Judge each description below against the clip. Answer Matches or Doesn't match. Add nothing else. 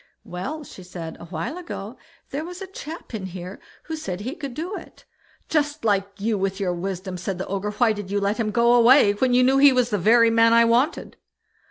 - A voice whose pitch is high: Matches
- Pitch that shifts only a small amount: Doesn't match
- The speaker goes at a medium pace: Doesn't match